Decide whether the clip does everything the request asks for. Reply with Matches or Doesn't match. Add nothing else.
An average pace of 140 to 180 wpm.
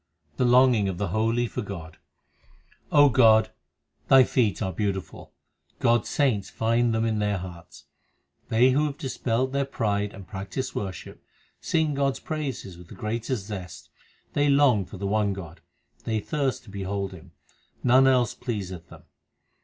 Matches